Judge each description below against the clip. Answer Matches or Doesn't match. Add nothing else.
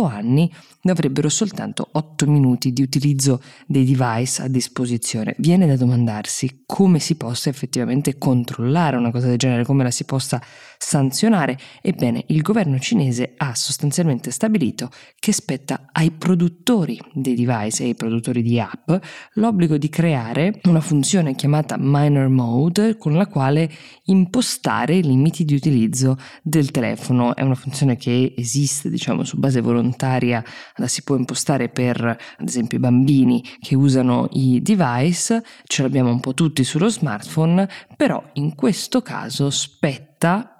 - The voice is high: Doesn't match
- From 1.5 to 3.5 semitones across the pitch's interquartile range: Doesn't match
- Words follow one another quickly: Doesn't match